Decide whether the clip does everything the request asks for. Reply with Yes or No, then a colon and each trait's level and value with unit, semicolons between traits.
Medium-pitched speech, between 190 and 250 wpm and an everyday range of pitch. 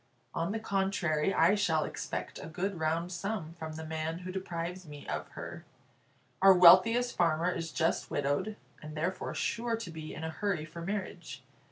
No: medium, 170 Hz; average, 175 wpm; average, 3.4 semitones